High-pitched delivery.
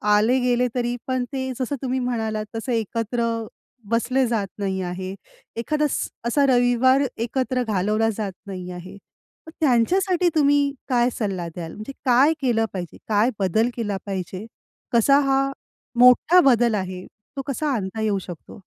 Yes: high, 235 Hz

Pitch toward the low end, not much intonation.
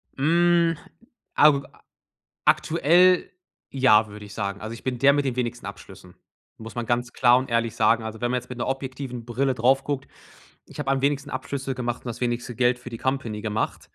No: low, 125 Hz; average, 3.0 semitones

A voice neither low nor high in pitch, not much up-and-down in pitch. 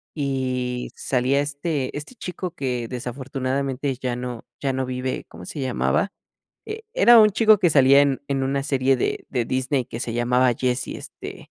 No: low, 130 Hz; narrow, 2.2 semitones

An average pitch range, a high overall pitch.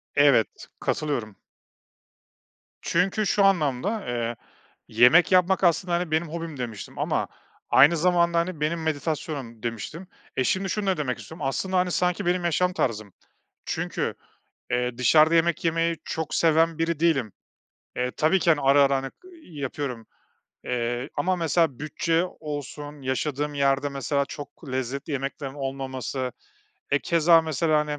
No: average, 4.1 semitones; medium, 150 Hz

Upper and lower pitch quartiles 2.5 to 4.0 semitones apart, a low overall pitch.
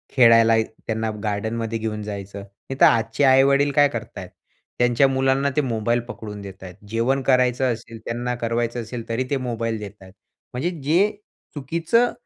Yes: average, 3.1 semitones; low, 120 Hz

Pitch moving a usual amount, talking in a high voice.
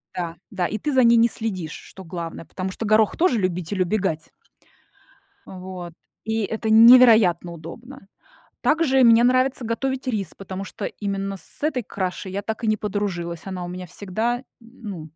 Yes: average, 4.3 semitones; high, 205 Hz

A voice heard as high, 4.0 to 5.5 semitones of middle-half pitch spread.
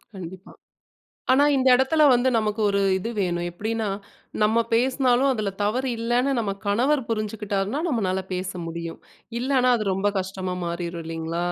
Yes: high, 210 Hz; average, 5.0 semitones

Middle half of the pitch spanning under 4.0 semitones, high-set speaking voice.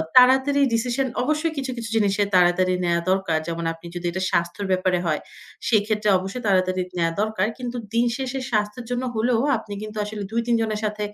No: average, 4.6 semitones; high, 210 Hz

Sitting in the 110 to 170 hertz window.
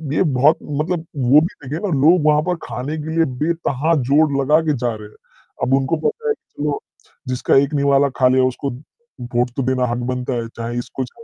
Yes: medium, 140 Hz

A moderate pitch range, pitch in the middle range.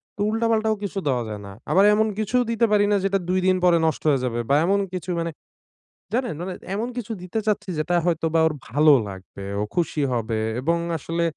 No: wide, 5.7 semitones; medium, 175 Hz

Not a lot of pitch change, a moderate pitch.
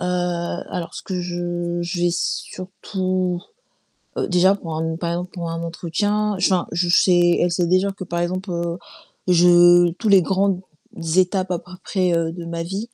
Yes: narrow, 1.4 semitones; medium, 175 Hz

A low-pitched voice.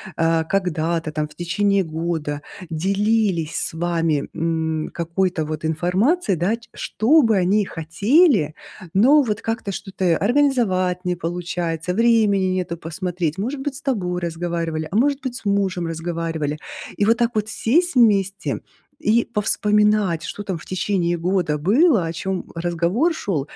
No: medium, 185 Hz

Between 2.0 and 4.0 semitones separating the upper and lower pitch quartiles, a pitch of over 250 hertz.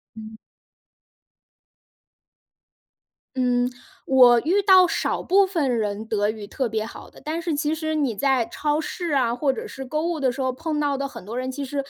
No: average, 4.5 semitones; very high, 270 Hz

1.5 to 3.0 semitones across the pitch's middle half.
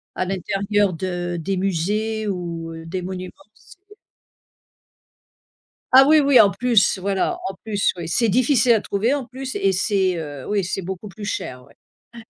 No: average, 3.6 semitones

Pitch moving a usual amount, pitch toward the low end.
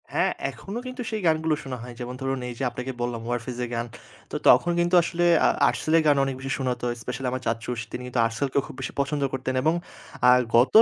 Yes: average, 3.8 semitones; low, 130 Hz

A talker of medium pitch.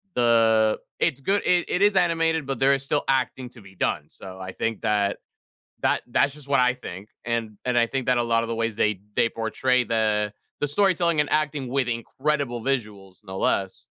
No: low, 120 Hz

